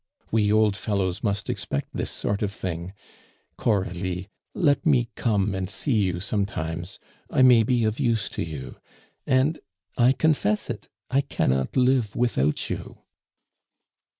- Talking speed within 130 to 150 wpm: Yes, average, 140 wpm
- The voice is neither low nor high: No, low, 105 Hz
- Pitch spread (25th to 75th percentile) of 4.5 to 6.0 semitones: Yes, average, 4.9 semitones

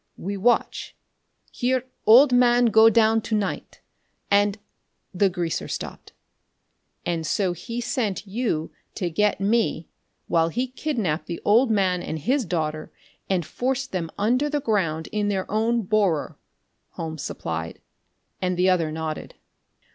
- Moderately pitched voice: No, high, 205 Hz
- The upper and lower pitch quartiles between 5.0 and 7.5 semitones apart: Yes, wide, 5.4 semitones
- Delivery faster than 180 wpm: No, average, 140 wpm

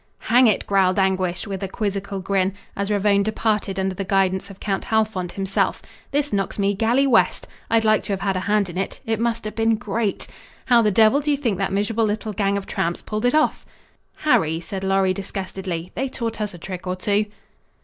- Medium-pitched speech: No, high, 200 Hz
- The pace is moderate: No, fast, 210 wpm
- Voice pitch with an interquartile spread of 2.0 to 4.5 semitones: Yes, narrow, 2.5 semitones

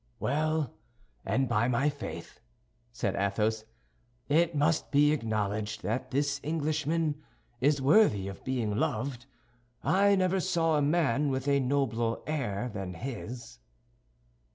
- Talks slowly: Yes, slow, 125 wpm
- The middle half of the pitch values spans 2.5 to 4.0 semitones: No, average, 5.1 semitones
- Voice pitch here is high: No, medium, 140 Hz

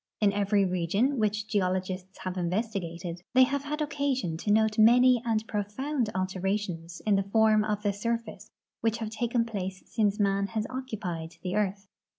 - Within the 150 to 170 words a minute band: Yes, average, 165 wpm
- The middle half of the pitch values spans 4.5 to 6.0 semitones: No, average, 3.3 semitones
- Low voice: No, high, 210 Hz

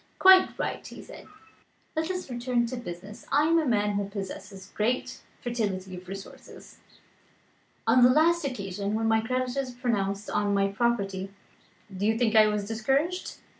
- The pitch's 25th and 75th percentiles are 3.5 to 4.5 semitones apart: Yes, average, 4.2 semitones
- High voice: Yes, high, 225 Hz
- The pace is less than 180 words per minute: Yes, average, 160 wpm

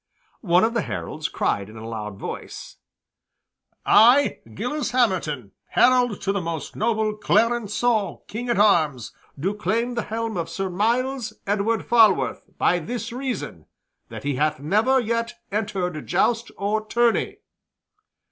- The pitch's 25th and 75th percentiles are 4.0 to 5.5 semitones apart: Yes, average, 4.9 semitones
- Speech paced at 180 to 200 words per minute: No, average, 140 wpm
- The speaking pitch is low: No, high, 215 Hz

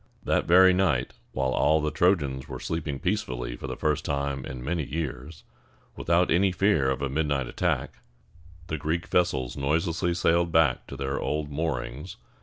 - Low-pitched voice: Yes, very low, 75 Hz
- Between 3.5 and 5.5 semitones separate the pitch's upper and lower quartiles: Yes, average, 4.0 semitones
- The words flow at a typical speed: Yes, average, 165 wpm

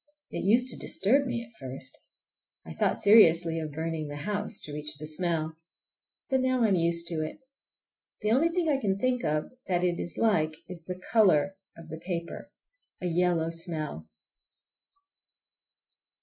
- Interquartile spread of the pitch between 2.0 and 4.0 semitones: No, average, 5.3 semitones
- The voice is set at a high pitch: No, medium, 170 Hz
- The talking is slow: No, average, 165 wpm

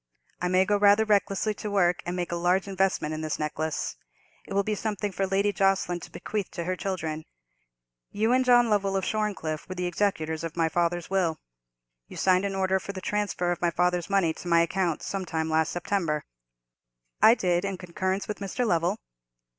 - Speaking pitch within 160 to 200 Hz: Yes, medium, 185 Hz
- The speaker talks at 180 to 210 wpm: Yes, average, 200 wpm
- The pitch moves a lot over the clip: No, average, 2.7 semitones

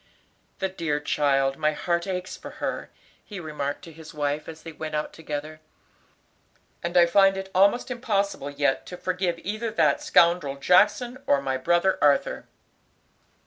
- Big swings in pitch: No, average, 4.5 semitones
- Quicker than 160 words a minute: No, average, 155 wpm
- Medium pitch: Yes, medium, 170 Hz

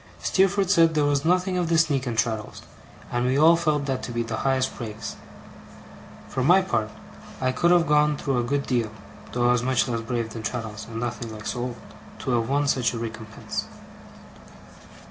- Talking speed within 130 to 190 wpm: No, average, 200 wpm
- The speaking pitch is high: No, low, 130 Hz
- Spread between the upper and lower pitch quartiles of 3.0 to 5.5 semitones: Yes, average, 4.4 semitones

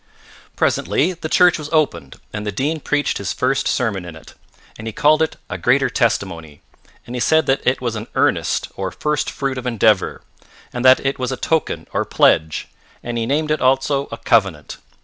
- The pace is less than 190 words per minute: No, average, 195 wpm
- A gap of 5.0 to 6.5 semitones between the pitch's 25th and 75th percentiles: Yes, wide, 5.6 semitones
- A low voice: Yes, low, 125 Hz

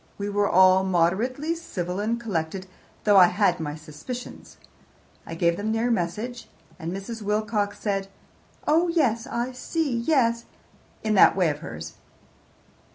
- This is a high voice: Yes, high, 205 Hz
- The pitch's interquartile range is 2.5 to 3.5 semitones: No, average, 4.8 semitones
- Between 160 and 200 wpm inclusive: No, average, 145 wpm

